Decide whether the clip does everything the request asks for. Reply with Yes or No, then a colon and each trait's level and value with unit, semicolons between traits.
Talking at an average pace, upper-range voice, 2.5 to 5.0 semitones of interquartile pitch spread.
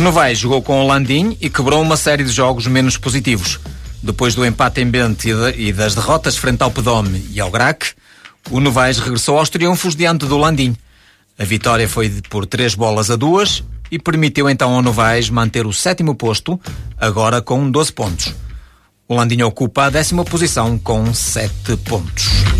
No: average, 175 wpm; low, 125 Hz; average, 4.3 semitones